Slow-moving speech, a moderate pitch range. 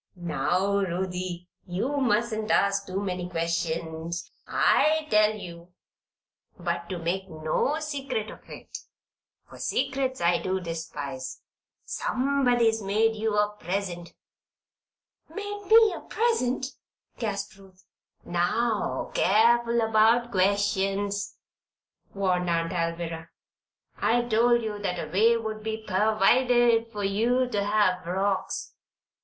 Yes: slow, 115 wpm; average, 4.6 semitones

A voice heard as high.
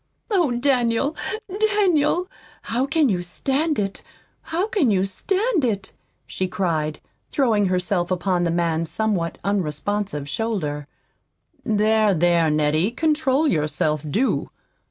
Yes: high, 205 Hz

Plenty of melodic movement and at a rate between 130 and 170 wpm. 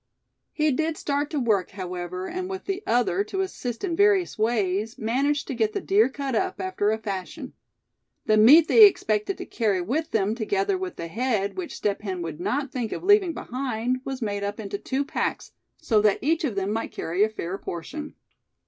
No: wide, 7.2 semitones; average, 200 wpm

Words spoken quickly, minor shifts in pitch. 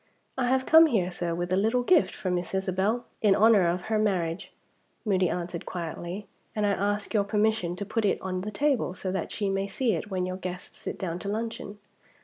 No: fast, 215 wpm; average, 3.2 semitones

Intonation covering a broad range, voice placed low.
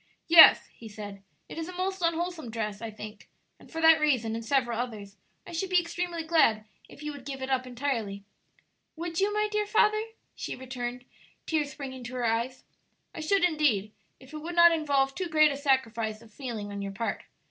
No: wide, 6.4 semitones; very high, 270 Hz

